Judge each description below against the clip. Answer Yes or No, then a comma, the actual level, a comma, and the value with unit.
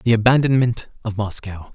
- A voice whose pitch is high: No, low, 115 Hz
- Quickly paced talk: No, average, 140 wpm